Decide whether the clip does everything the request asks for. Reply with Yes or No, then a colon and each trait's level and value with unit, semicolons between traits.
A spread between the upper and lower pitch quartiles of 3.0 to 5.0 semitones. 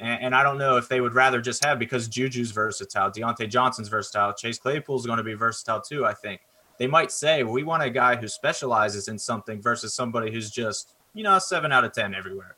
No: narrow, 2.5 semitones